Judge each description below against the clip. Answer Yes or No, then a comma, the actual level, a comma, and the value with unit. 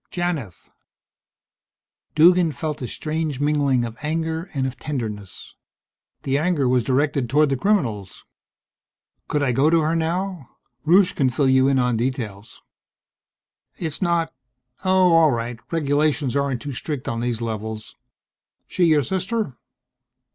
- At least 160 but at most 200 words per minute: No, slow, 135 wpm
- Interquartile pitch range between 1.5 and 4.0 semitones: No, average, 4.7 semitones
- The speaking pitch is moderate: Yes, medium, 145 Hz